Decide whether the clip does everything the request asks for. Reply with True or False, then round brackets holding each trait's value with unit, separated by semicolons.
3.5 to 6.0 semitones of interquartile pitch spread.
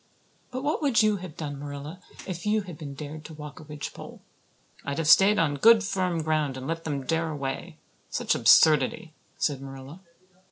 True (4.3 semitones)